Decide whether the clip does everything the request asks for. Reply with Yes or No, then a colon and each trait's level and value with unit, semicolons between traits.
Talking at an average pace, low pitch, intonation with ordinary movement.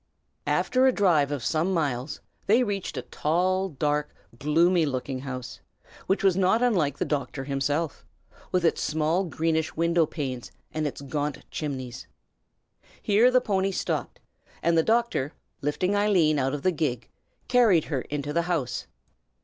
No: average, 150 wpm; medium, 160 Hz; average, 4.6 semitones